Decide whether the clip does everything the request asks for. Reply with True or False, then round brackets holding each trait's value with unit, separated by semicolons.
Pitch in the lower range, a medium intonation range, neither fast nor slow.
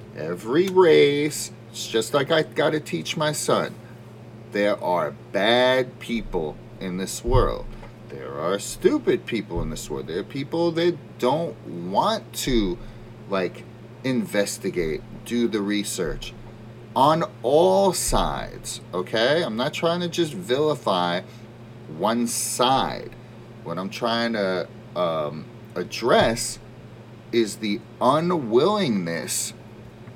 False (115 Hz; 4.8 semitones; 115 wpm)